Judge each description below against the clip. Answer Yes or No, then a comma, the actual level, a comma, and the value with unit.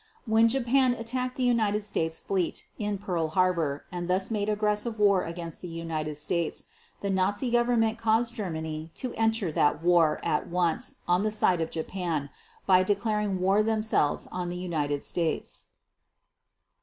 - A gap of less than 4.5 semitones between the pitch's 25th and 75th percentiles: No, average, 4.8 semitones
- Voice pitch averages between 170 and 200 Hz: Yes, high, 190 Hz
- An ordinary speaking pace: Yes, average, 155 wpm